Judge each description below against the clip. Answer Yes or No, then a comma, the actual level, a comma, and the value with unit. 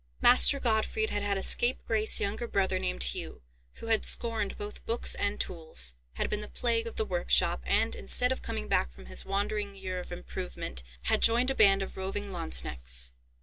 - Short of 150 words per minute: No, average, 190 wpm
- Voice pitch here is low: No, high, 195 Hz